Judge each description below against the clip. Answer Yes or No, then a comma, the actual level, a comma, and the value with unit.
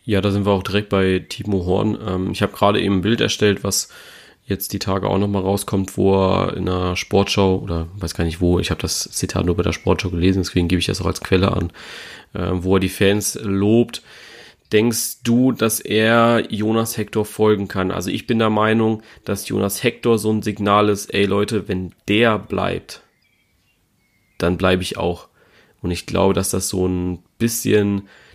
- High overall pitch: No, low, 100 Hz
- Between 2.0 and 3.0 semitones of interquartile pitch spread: Yes, narrow, 2.5 semitones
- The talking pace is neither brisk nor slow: No, fast, 200 wpm